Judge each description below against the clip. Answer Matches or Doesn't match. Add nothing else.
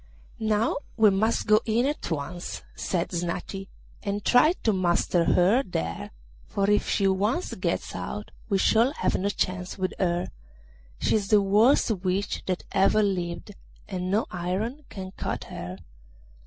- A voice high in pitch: Matches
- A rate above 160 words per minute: Doesn't match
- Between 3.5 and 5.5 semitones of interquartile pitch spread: Doesn't match